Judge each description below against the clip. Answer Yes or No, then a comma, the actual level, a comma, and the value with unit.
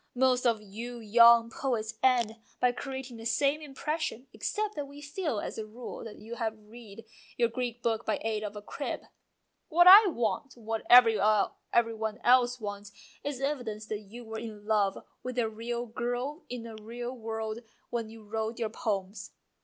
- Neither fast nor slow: Yes, average, 180 wpm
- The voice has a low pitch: No, high, 230 Hz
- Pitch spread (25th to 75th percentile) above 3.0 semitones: No, narrow, 2.4 semitones